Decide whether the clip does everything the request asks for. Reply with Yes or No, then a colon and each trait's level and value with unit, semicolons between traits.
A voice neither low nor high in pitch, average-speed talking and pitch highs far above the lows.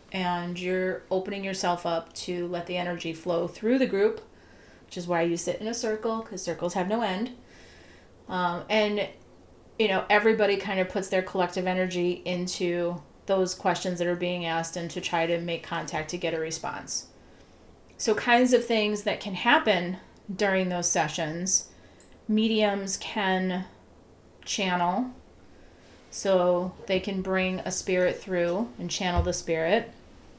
No: medium, 180 Hz; average, 155 wpm; average, 2.8 semitones